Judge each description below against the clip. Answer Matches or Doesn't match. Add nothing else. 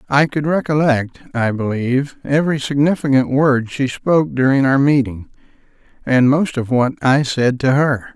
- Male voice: Matches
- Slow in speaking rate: Doesn't match